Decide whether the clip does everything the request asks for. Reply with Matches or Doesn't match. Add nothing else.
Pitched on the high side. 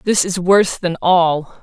Doesn't match